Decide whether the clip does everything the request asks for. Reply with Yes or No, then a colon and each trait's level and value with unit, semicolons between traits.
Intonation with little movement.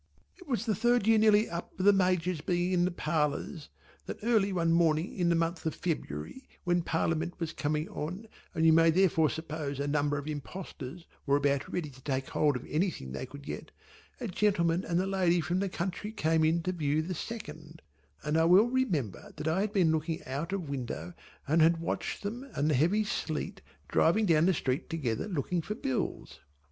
No: average, 3.8 semitones